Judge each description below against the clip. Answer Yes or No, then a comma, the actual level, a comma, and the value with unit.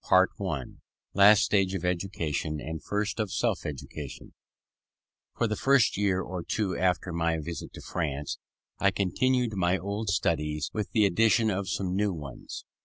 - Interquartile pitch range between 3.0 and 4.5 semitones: Yes, average, 3.8 semitones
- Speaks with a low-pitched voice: Yes, very low, 95 Hz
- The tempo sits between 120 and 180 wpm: Yes, average, 160 wpm